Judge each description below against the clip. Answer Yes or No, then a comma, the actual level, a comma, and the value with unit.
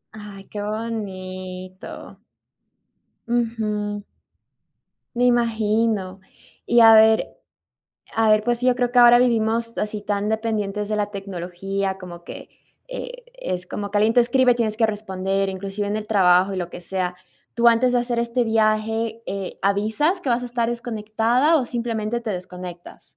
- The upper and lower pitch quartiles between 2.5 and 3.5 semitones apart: Yes, average, 3.1 semitones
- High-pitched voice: Yes, high, 215 Hz